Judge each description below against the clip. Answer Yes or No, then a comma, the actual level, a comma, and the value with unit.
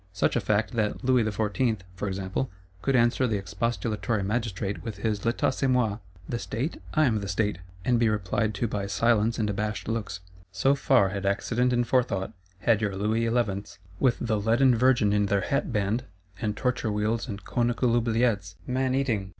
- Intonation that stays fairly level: No, average, 3.0 semitones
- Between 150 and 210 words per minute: Yes, average, 180 wpm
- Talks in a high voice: No, low, 110 Hz